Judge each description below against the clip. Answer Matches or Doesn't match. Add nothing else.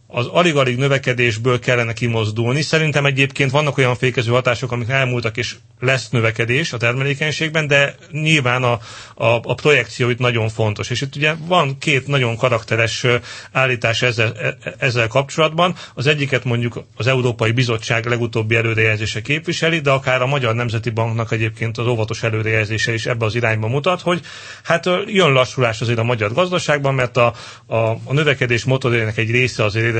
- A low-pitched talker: Matches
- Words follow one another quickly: Matches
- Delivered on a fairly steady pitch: Doesn't match